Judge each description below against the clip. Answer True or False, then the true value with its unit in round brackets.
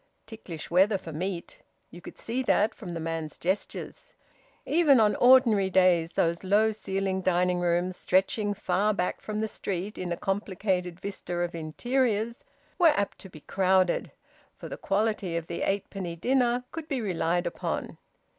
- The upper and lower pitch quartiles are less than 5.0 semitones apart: True (3.6 semitones)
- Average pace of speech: True (160 wpm)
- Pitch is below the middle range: False (190 Hz)